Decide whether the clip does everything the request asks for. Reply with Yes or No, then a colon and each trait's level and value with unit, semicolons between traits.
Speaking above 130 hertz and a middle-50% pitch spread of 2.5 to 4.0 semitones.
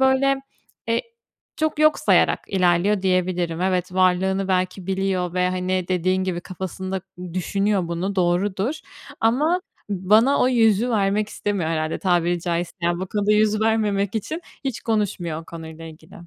Yes: high, 190 Hz; average, 3.1 semitones